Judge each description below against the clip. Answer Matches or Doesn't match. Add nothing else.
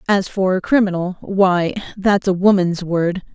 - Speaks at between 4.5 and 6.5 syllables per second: Doesn't match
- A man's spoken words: Doesn't match